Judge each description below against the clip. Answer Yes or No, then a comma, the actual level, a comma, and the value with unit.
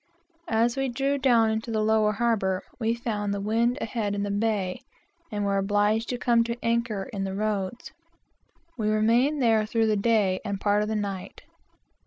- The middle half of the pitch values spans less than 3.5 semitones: Yes, narrow, 2.4 semitones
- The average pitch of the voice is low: No, high, 220 Hz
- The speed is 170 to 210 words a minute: Yes, average, 190 wpm